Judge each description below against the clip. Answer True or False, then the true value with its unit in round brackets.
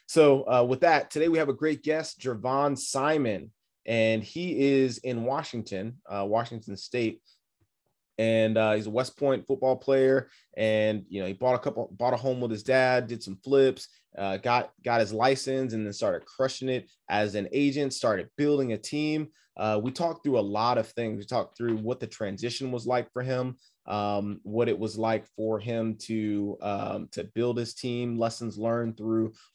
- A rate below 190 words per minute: False (195 wpm)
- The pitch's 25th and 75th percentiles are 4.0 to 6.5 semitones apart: False (3.3 semitones)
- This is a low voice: True (120 Hz)